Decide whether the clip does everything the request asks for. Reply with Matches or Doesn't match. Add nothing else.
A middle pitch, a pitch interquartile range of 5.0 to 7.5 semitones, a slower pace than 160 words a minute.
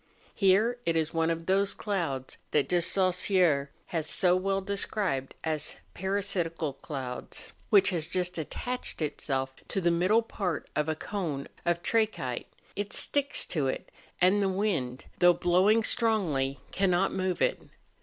Doesn't match